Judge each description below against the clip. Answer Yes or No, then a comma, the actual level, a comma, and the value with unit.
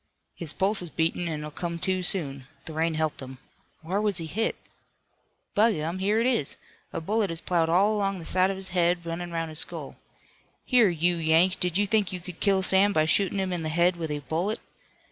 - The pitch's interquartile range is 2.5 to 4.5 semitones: Yes, average, 3.2 semitones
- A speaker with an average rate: No, fast, 220 wpm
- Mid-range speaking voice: Yes, medium, 175 Hz